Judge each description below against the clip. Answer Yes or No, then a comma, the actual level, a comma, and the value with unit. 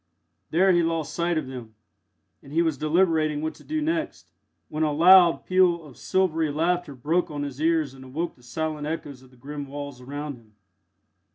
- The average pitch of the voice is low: No, medium, 155 Hz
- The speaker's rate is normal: Yes, average, 190 wpm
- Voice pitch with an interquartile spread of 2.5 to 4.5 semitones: Yes, average, 3.1 semitones